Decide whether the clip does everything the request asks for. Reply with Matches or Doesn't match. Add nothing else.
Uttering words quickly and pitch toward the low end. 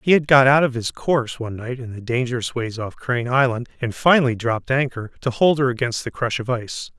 Matches